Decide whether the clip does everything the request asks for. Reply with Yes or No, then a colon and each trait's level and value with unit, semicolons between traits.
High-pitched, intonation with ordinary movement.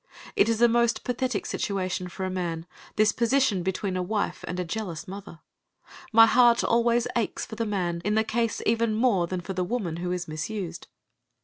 Yes: high, 205 Hz; average, 4.4 semitones